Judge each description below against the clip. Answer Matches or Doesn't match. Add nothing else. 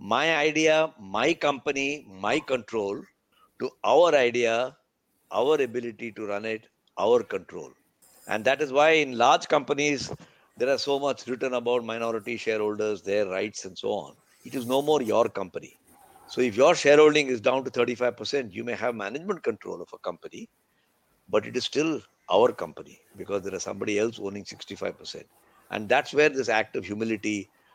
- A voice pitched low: Matches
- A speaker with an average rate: Matches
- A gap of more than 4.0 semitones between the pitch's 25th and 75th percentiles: Matches